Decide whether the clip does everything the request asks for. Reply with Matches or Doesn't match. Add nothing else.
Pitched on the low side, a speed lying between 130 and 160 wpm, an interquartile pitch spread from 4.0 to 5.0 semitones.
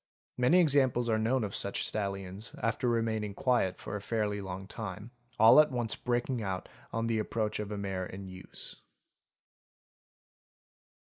Doesn't match